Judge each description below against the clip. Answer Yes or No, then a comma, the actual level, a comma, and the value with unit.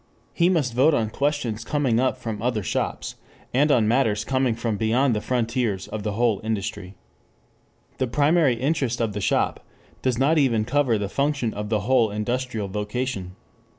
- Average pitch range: Yes, average, 3.7 semitones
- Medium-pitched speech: No, low, 120 Hz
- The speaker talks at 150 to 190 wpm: Yes, average, 170 wpm